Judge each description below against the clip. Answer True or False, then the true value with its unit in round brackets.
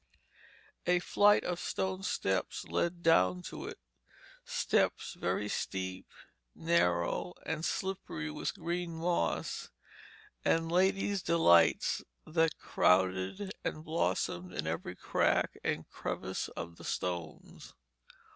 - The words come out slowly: True (110 wpm)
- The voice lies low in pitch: False (160 Hz)